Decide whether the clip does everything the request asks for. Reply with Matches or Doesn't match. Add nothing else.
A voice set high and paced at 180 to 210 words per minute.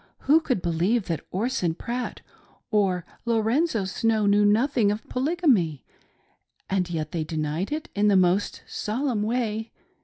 Doesn't match